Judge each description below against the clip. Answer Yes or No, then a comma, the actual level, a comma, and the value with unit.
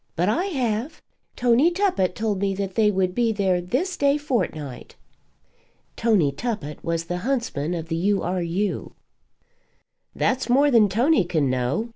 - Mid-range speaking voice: No, high, 205 Hz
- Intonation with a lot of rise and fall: Yes, wide, 5.8 semitones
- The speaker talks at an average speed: Yes, average, 155 wpm